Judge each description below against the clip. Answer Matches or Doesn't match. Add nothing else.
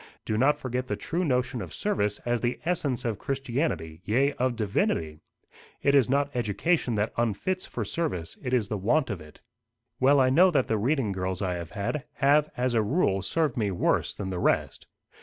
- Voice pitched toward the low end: Matches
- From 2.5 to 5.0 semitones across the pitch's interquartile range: Doesn't match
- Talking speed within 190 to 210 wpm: Matches